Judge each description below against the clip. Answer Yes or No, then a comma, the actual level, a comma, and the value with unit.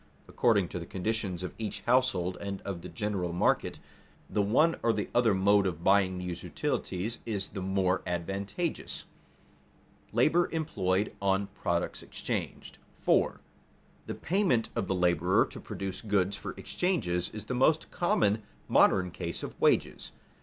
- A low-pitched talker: Yes, low, 100 Hz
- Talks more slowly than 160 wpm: Yes, average, 150 wpm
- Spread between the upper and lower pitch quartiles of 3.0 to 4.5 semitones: Yes, average, 3.6 semitones